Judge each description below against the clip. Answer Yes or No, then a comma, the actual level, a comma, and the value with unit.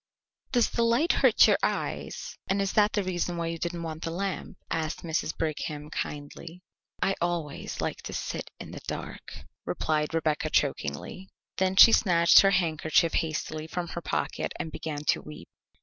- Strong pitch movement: No, average, 3.0 semitones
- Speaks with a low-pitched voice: No, medium, 170 Hz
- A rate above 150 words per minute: Yes, average, 170 wpm